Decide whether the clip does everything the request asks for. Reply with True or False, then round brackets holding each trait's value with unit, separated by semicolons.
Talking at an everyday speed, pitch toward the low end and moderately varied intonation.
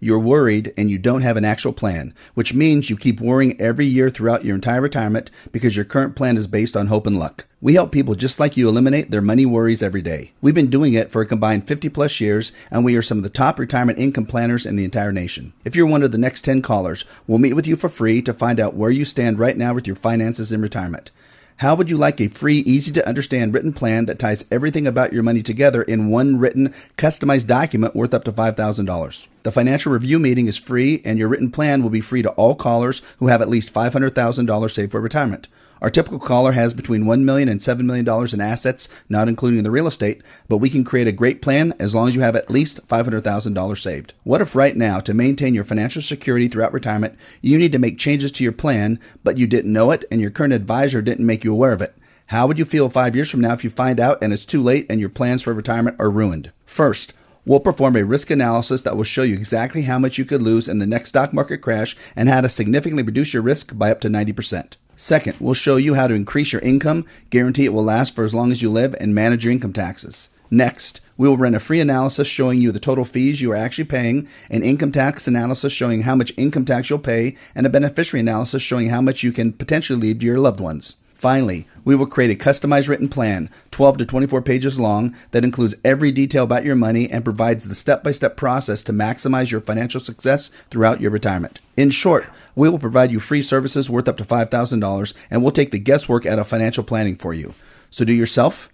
False (240 wpm; 120 Hz; 3.4 semitones)